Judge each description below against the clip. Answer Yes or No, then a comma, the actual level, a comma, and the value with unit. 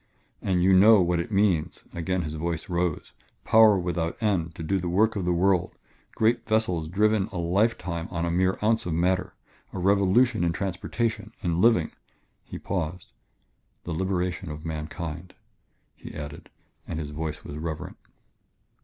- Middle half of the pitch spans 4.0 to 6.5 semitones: No, average, 3.0 semitones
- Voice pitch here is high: No, very low, 90 Hz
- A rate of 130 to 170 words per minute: Yes, average, 160 wpm